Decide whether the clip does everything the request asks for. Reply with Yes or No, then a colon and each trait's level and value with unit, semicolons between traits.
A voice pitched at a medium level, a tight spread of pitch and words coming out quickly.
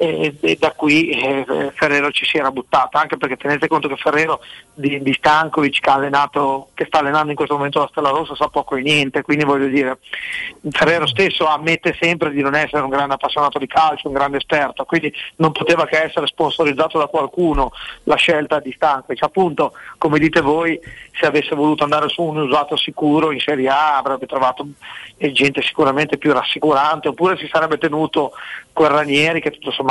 Yes: medium, 150 Hz; narrow, 2.0 semitones; fast, 185 wpm